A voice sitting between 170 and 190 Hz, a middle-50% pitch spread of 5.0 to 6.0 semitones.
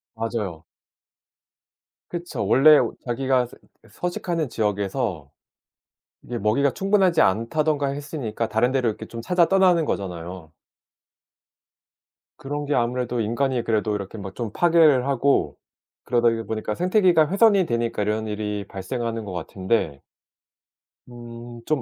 No: low, 120 Hz; wide, 5.5 semitones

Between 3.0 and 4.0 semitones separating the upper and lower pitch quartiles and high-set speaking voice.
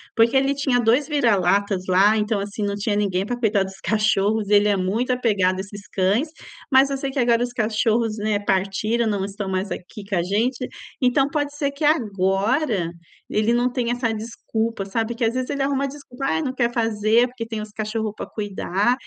Yes: average, 3.4 semitones; high, 220 Hz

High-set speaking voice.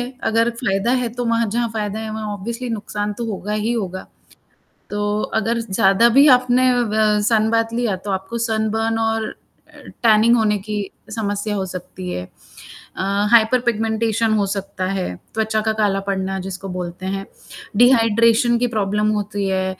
Yes: high, 215 Hz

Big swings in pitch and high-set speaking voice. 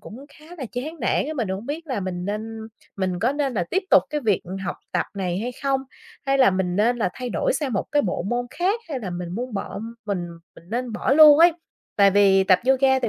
Yes: wide, 6.0 semitones; high, 240 Hz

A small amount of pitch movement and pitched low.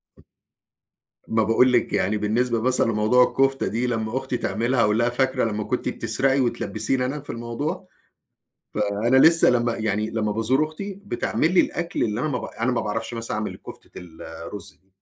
No: average, 3.5 semitones; low, 120 Hz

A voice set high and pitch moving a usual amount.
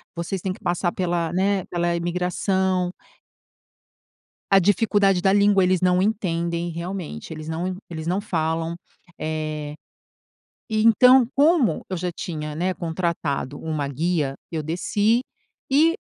No: medium, 175 Hz; average, 3.1 semitones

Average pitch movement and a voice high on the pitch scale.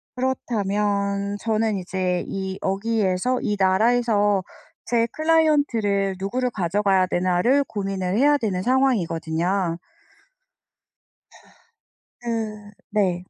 Yes: average, 3.7 semitones; high, 205 Hz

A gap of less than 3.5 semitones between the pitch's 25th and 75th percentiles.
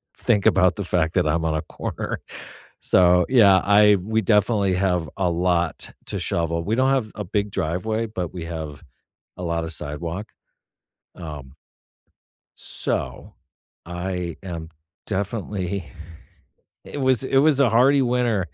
No: average, 4.3 semitones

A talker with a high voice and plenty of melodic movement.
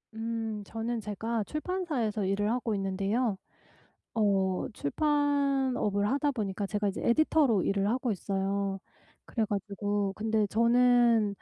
No: high, 220 Hz; average, 3.4 semitones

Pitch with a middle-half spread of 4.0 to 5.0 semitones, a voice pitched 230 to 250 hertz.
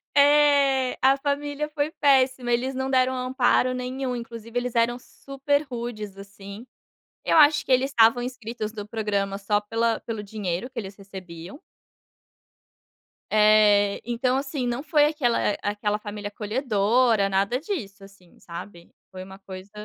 Yes: average, 4.4 semitones; high, 235 Hz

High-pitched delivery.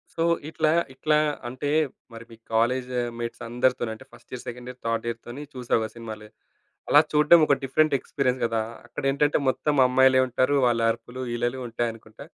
No: low, 125 Hz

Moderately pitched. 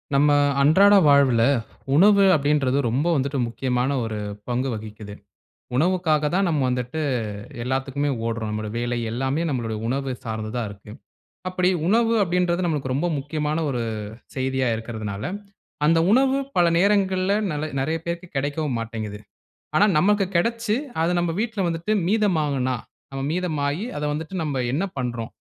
Yes: medium, 145 Hz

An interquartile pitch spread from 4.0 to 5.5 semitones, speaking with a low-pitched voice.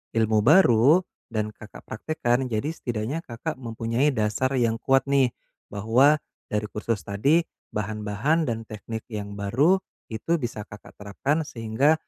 Yes: average, 4.6 semitones; low, 115 Hz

